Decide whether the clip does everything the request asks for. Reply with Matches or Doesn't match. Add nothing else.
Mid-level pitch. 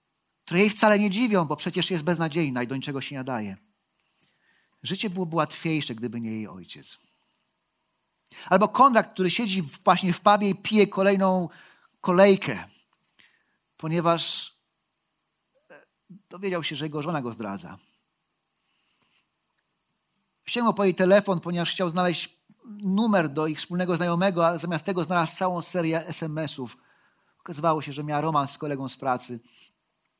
Matches